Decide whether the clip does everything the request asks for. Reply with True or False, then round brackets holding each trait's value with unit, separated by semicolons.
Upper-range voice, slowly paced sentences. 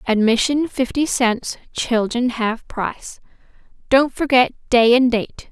True (245 Hz; 120 wpm)